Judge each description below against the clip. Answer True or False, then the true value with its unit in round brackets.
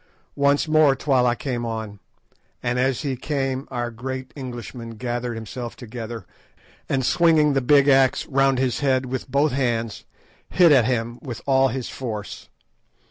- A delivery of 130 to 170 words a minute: True (150 wpm)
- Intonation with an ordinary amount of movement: False (2.3 semitones)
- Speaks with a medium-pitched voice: False (130 Hz)